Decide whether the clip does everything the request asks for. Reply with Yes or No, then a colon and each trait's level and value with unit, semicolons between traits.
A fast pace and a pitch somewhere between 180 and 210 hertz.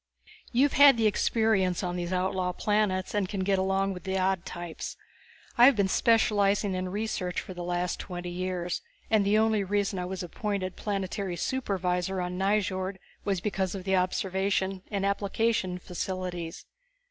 No: average, 160 wpm; high, 190 Hz